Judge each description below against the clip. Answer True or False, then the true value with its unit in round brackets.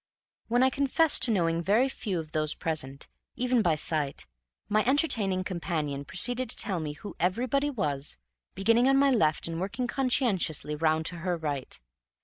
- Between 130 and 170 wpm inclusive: True (165 wpm)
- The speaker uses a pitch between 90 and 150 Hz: False (185 Hz)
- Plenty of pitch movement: True (7.7 semitones)